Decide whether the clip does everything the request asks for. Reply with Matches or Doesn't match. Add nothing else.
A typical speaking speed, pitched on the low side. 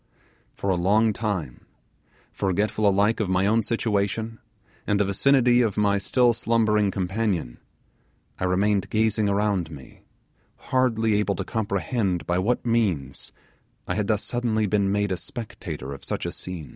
Matches